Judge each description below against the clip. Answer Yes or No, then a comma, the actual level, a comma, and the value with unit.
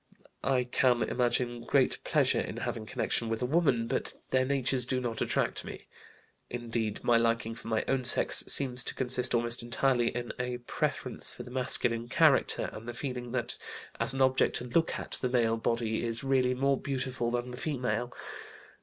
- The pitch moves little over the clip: Yes, narrow, 1.7 semitones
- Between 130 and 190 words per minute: Yes, average, 180 wpm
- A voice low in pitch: Yes, low, 125 Hz